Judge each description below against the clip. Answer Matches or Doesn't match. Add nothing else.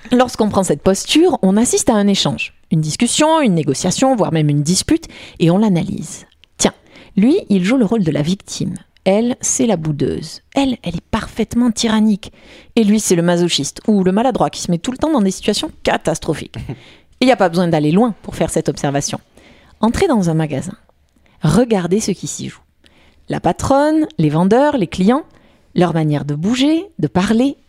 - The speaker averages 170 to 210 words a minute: Matches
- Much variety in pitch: Matches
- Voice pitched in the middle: Doesn't match